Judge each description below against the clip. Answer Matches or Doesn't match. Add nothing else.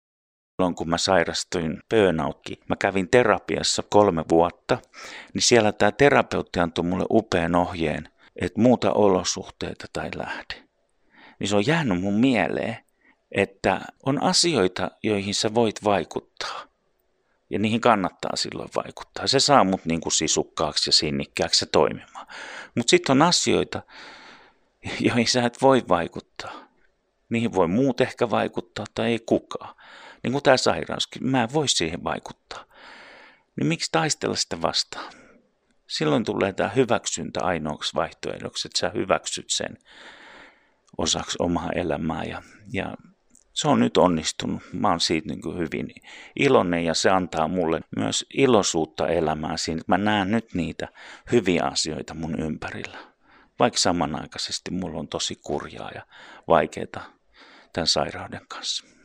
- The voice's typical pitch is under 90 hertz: Doesn't match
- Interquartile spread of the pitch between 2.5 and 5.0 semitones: Doesn't match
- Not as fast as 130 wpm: Doesn't match